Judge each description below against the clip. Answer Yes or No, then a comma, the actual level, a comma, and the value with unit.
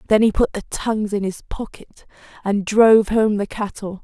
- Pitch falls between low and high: No, high, 210 Hz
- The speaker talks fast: No, average, 195 wpm